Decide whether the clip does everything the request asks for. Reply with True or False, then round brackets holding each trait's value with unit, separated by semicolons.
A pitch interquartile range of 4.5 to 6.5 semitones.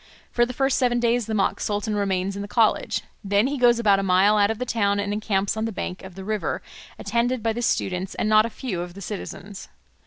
False (2.9 semitones)